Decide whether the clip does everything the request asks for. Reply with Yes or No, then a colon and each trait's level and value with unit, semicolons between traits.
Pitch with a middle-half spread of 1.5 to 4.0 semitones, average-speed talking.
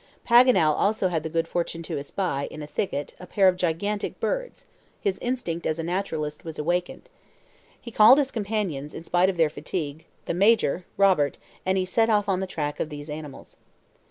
No: average, 4.6 semitones; average, 195 wpm